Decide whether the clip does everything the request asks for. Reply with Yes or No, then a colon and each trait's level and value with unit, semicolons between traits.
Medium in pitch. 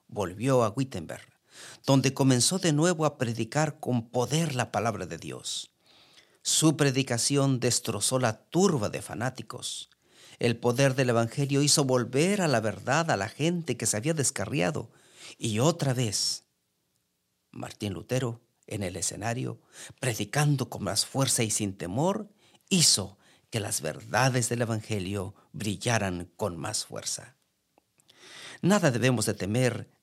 No: low, 125 Hz